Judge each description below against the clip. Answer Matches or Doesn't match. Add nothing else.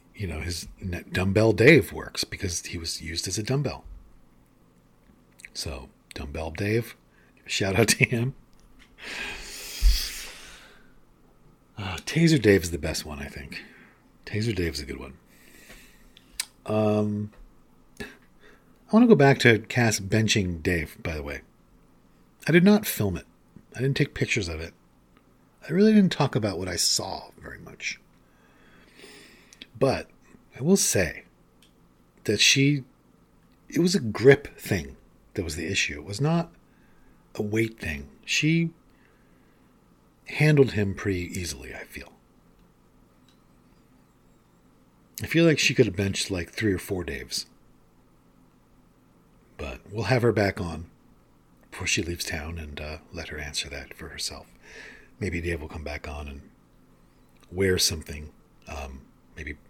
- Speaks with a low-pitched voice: Matches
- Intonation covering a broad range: Matches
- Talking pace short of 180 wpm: Matches